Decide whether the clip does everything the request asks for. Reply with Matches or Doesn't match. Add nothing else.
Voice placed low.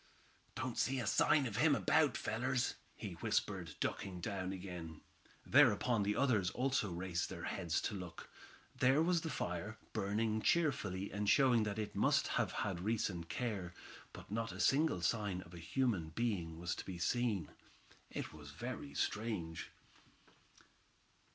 Matches